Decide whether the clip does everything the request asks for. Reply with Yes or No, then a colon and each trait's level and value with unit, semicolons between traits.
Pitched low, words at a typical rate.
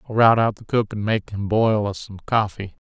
No: low, 105 Hz; fast, 250 wpm